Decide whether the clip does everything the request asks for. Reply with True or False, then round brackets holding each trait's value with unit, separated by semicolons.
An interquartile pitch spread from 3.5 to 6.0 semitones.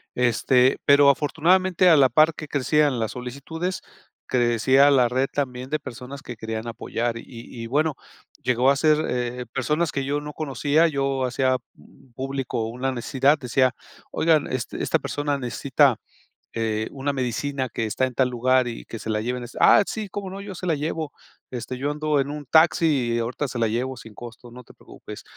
False (3.1 semitones)